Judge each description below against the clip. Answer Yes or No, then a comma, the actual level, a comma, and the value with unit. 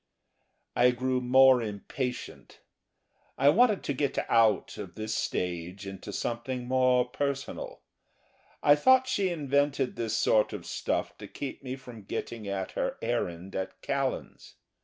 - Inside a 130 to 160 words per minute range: Yes, average, 140 wpm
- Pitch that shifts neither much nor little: Yes, average, 4.3 semitones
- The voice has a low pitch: Yes, low, 125 Hz